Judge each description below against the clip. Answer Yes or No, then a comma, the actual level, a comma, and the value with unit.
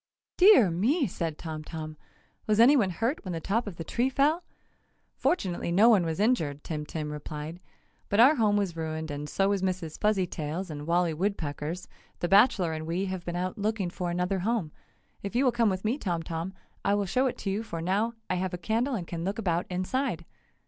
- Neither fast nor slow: No, fast, 210 wpm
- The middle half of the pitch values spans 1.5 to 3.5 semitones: No, average, 4.8 semitones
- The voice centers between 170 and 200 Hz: Yes, medium, 185 Hz